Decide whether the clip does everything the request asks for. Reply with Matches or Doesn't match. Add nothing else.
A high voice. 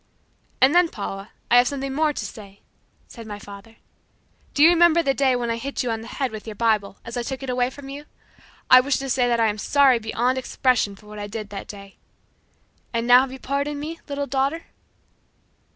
Matches